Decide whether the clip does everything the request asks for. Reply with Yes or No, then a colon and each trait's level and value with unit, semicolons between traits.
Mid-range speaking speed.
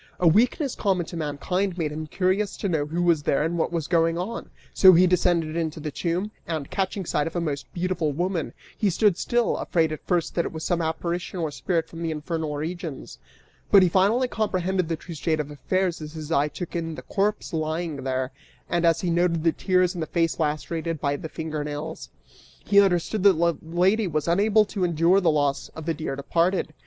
No: fast, 215 wpm